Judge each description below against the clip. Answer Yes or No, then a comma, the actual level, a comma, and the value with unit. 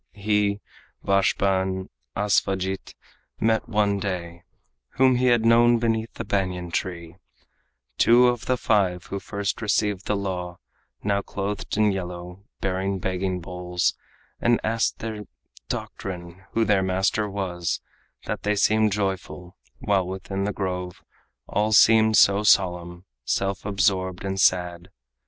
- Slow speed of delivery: Yes, slow, 130 wpm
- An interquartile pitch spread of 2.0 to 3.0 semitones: Yes, narrow, 2.4 semitones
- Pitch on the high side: No, low, 100 Hz